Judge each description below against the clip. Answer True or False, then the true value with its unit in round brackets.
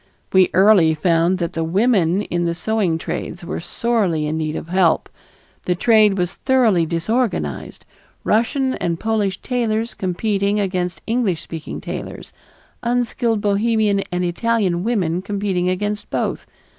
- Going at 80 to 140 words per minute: True (135 wpm)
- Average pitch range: True (4.3 semitones)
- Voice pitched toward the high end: True (195 Hz)